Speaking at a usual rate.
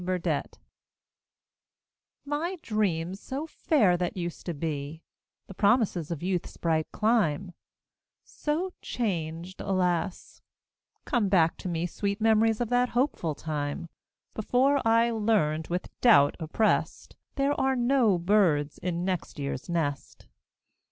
No: slow, 120 wpm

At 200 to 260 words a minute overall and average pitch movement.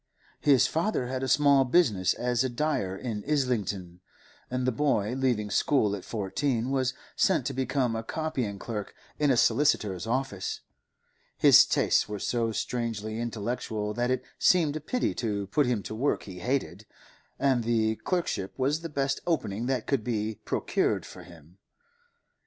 No: average, 160 wpm; average, 4.4 semitones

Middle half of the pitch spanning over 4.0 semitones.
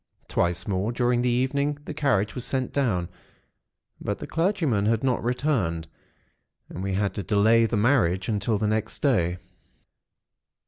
Yes: average, 4.9 semitones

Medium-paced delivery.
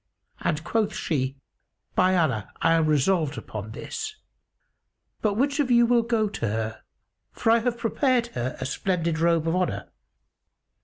Yes: average, 155 wpm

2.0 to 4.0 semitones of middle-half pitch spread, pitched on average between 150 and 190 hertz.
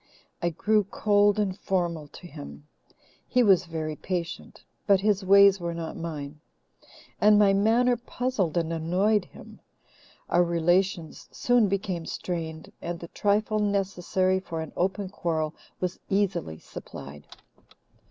Yes: average, 3.5 semitones; medium, 185 Hz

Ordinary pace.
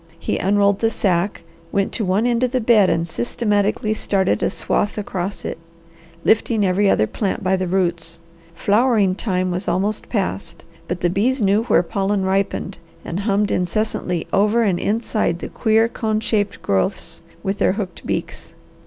Yes: average, 165 wpm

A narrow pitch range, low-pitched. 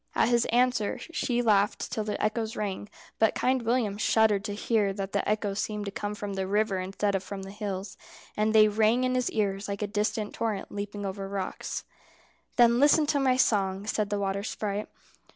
No: narrow, 1.9 semitones; high, 210 Hz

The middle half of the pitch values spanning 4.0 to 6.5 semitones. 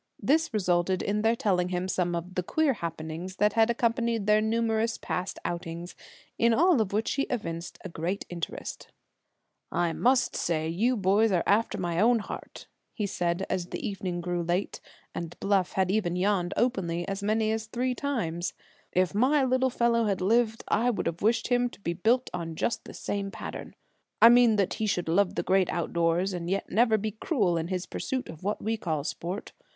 Yes: average, 4.6 semitones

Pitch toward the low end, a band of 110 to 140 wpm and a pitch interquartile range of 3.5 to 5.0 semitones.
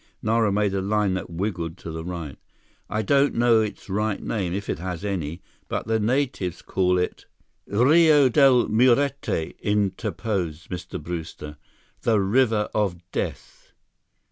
Yes: low, 100 Hz; slow, 135 wpm; average, 4.2 semitones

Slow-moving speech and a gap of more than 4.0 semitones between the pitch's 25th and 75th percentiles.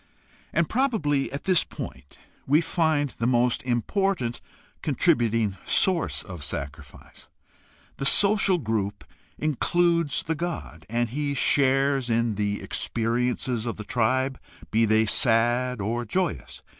Yes: slow, 120 wpm; average, 5.0 semitones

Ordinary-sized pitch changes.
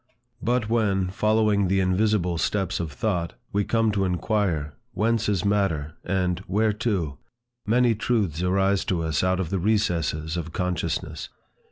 Yes: average, 3.5 semitones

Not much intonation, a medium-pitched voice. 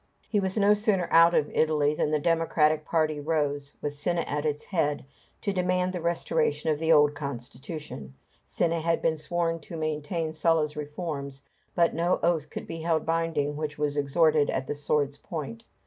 Yes: narrow, 2.3 semitones; medium, 155 Hz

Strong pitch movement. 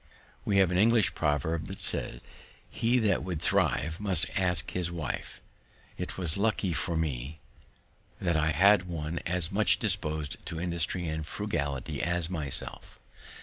No: average, 3.4 semitones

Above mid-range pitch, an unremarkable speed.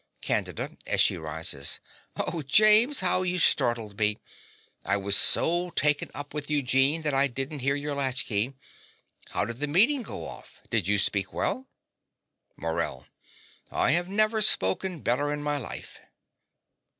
No: medium, 145 Hz; average, 150 wpm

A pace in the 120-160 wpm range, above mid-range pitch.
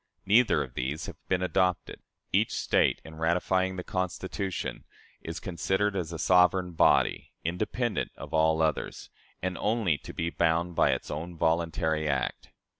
No: average, 150 wpm; very low, 85 Hz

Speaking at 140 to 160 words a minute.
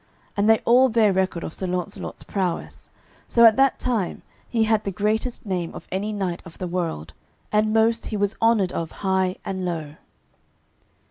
No: average, 180 wpm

